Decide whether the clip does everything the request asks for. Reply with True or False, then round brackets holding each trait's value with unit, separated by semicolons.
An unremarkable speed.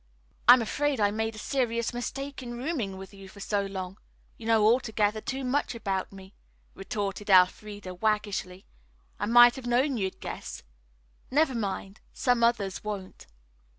True (150 wpm)